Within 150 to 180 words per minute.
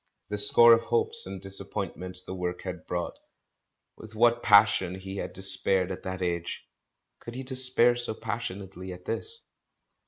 Yes: average, 160 wpm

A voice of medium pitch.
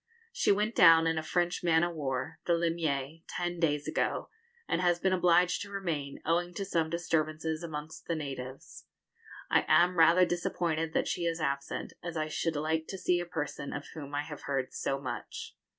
Yes: medium, 165 Hz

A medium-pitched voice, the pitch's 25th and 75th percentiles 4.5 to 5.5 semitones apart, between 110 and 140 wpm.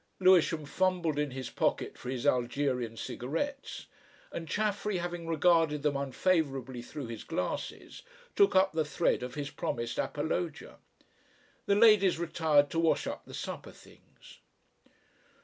Yes: medium, 155 Hz; average, 4.8 semitones; slow, 135 wpm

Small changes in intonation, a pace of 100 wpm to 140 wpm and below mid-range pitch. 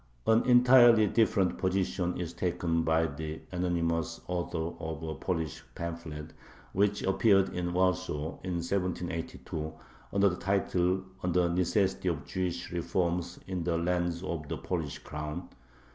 Yes: narrow, 2.0 semitones; slow, 135 wpm; very low, 90 Hz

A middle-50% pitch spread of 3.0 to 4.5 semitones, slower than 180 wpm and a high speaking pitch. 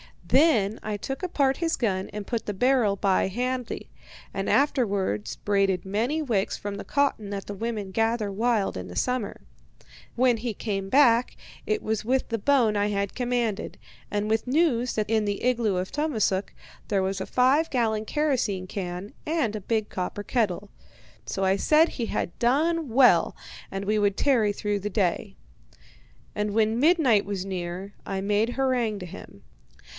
Yes: average, 4.1 semitones; average, 170 wpm; high, 215 Hz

